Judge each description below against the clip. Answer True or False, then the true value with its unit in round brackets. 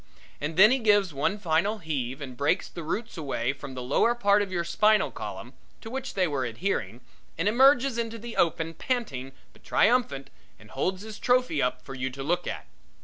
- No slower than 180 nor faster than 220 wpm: True (200 wpm)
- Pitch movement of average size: False (8.1 semitones)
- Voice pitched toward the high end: False (175 Hz)